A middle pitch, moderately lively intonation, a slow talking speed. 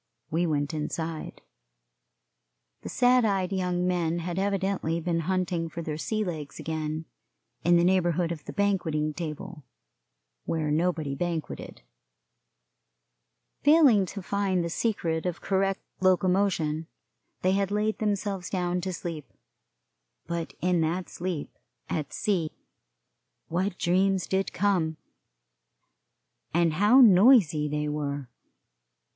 Yes: medium, 175 Hz; average, 3.2 semitones; slow, 115 wpm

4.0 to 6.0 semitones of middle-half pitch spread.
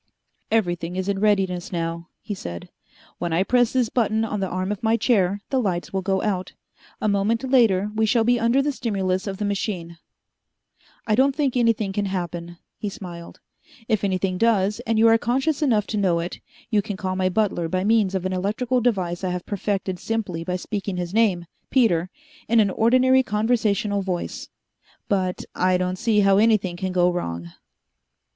No: average, 3.6 semitones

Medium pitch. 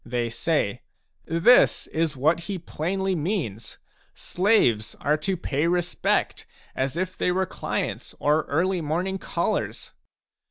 Yes: medium, 165 Hz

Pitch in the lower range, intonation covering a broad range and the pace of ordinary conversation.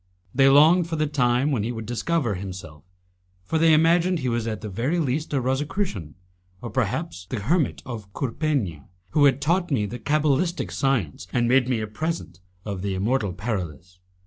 Yes: low, 125 Hz; wide, 7.1 semitones; average, 180 wpm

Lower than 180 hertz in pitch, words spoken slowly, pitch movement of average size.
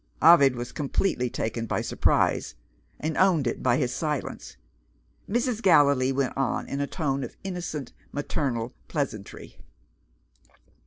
Yes: medium, 140 Hz; slow, 125 wpm; average, 4.2 semitones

